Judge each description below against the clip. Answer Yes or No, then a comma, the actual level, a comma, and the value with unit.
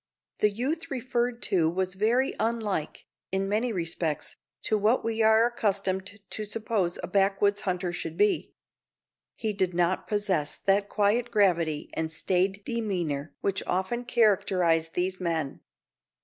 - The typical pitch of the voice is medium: No, high, 200 Hz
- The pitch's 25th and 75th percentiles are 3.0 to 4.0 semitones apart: Yes, average, 3.6 semitones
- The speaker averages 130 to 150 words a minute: Yes, slow, 135 wpm